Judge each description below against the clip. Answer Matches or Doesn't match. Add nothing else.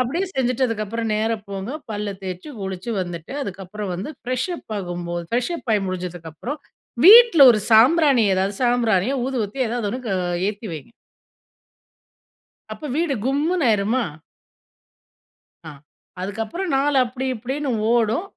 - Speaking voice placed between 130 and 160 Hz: Doesn't match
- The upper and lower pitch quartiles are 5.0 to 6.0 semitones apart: Matches